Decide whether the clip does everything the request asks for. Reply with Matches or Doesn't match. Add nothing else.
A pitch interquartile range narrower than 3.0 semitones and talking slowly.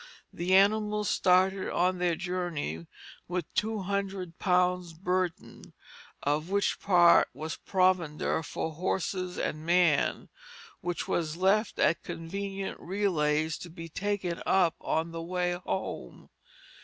Matches